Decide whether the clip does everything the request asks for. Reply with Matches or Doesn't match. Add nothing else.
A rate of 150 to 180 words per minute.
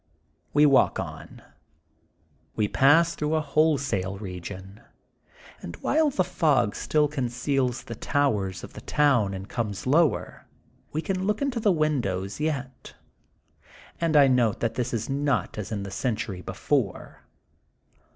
Doesn't match